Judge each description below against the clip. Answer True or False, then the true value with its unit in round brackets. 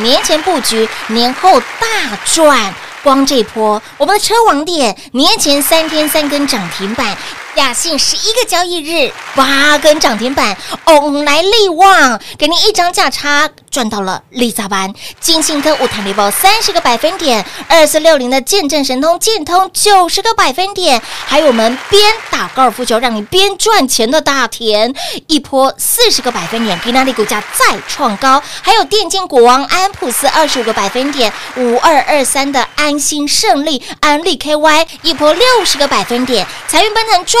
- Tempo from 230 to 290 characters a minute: True (260 characters per minute)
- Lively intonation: True (6.0 semitones)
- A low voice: False (295 Hz)